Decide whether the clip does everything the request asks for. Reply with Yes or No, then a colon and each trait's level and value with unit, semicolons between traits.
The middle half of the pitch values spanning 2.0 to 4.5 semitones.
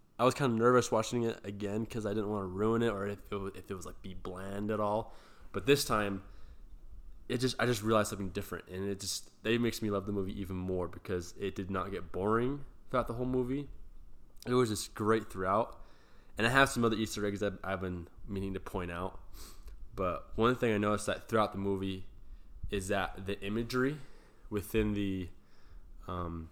Yes: average, 3.3 semitones